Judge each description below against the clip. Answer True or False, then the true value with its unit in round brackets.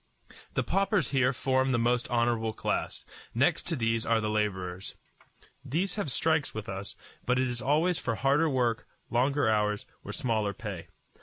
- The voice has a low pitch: True (120 Hz)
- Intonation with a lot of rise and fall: False (4.1 semitones)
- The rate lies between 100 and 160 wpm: False (170 wpm)